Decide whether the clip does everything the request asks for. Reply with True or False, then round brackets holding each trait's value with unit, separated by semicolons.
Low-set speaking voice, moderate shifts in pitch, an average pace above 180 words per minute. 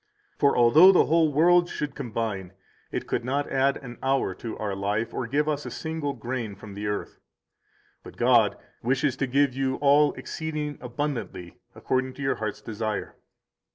False (130 Hz; 4.7 semitones; 170 wpm)